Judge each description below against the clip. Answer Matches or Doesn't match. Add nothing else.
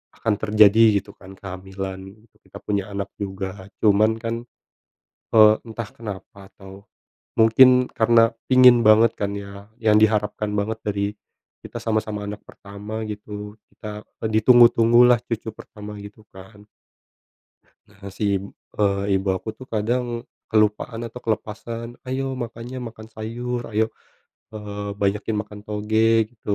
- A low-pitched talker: Matches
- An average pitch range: Doesn't match